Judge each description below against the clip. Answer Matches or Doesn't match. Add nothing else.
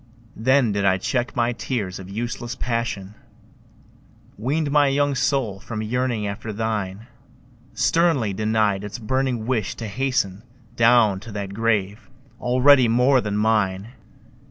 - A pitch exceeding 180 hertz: Doesn't match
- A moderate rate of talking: Doesn't match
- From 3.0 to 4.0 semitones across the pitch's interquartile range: Matches